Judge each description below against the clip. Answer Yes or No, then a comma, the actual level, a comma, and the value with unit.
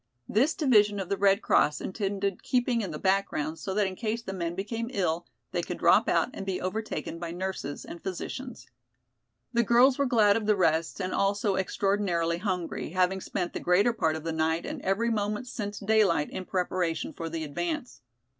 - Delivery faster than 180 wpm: Yes, average, 190 wpm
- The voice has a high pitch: Yes, high, 195 Hz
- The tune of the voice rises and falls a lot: No, average, 3.8 semitones